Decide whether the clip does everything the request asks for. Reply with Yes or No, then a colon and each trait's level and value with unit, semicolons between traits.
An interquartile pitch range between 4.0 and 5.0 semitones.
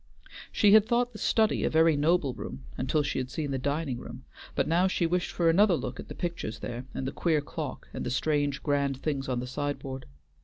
Yes: average, 4.3 semitones